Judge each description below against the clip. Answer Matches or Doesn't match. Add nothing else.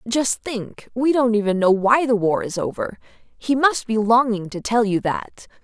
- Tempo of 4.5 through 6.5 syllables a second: Doesn't match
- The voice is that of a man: Doesn't match